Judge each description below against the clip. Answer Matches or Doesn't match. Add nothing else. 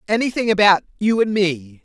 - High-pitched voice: Matches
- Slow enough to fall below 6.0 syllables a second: Matches